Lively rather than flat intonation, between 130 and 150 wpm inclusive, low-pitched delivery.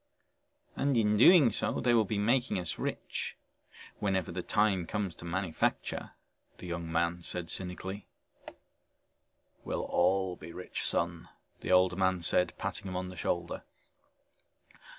No: average, 2.9 semitones; average, 140 wpm; very low, 95 Hz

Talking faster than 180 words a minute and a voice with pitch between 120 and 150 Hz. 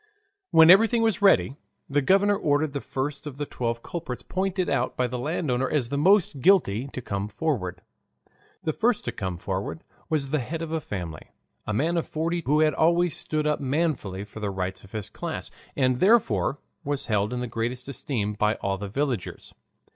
Yes: average, 190 wpm; medium, 140 Hz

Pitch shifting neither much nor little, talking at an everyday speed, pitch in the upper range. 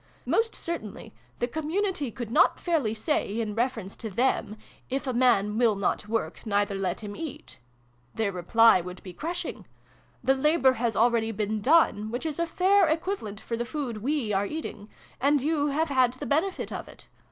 No: wide, 6.3 semitones; average, 185 wpm; high, 240 Hz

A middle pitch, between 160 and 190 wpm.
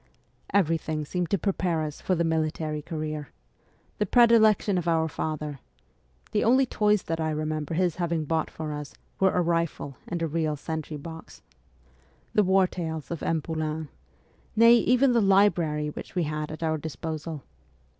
Yes: medium, 160 Hz; average, 165 wpm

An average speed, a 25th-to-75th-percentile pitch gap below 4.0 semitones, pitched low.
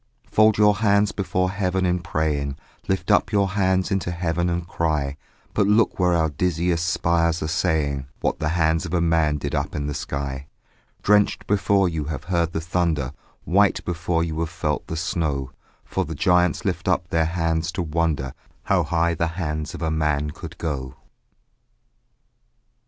Yes: average, 175 wpm; average, 2.7 semitones; very low, 85 Hz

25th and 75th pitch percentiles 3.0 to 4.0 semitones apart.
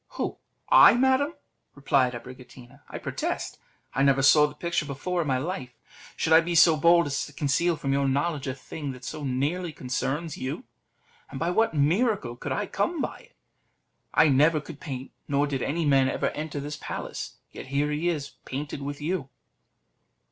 Yes: average, 3.7 semitones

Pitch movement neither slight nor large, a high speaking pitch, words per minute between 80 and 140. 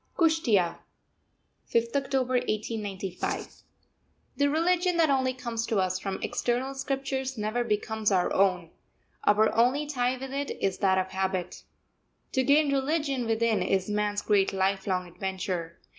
No: wide, 5.8 semitones; high, 230 Hz; slow, 135 wpm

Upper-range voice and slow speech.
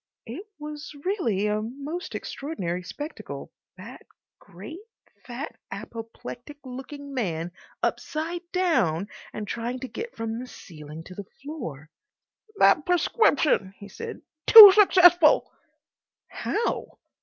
Yes: very high, 270 Hz; slow, 110 wpm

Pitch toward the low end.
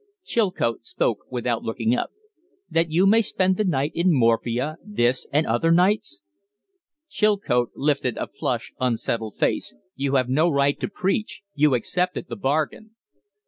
No: medium, 145 Hz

